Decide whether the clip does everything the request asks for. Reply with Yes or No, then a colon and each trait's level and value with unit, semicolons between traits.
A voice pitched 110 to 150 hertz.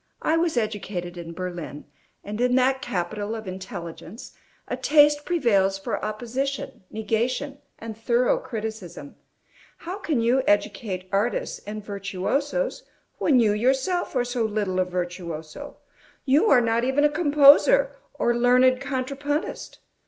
No: high, 235 Hz